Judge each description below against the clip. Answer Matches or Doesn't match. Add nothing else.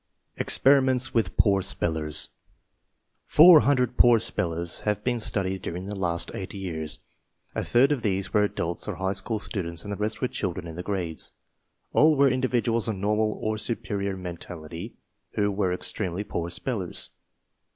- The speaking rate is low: Doesn't match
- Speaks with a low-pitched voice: Matches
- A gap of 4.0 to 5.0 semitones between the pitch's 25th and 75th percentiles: Matches